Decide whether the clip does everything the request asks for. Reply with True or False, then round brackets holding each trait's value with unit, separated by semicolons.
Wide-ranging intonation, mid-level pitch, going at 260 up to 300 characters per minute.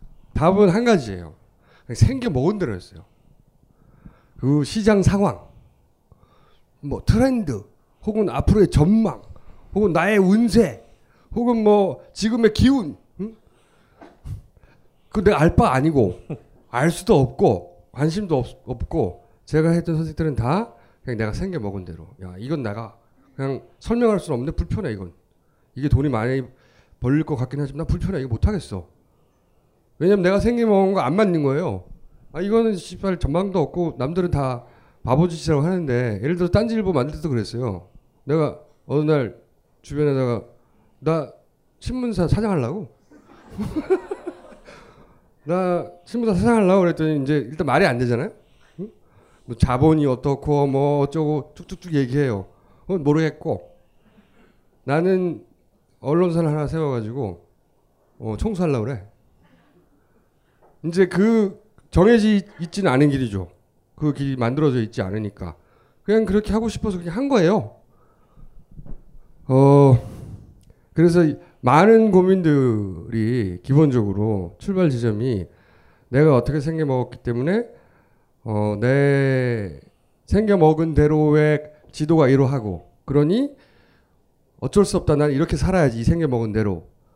True (7.2 semitones; 145 Hz; 270 characters per minute)